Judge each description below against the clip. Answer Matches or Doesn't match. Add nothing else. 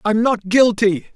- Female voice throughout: Doesn't match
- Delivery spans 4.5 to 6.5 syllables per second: Doesn't match